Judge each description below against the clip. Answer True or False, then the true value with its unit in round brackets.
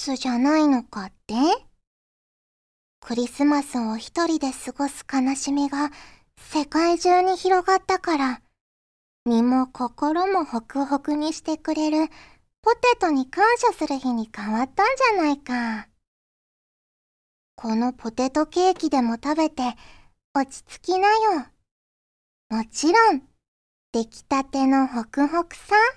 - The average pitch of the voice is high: True (285 Hz)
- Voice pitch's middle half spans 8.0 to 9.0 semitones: False (5.3 semitones)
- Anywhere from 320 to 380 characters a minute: False (235 characters per minute)